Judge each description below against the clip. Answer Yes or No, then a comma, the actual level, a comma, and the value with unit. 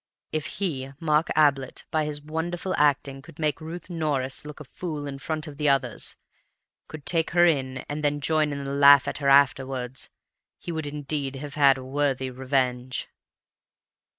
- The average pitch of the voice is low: No, medium, 145 Hz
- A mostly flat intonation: Yes, narrow, 2.3 semitones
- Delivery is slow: No, average, 175 wpm